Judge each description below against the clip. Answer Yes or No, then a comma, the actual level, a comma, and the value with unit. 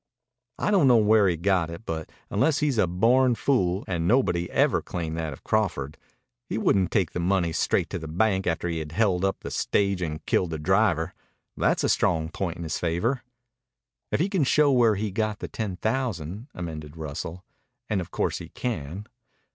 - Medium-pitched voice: No, very low, 95 Hz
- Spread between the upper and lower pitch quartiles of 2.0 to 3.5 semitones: No, average, 5.1 semitones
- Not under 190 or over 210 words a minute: Yes, average, 195 wpm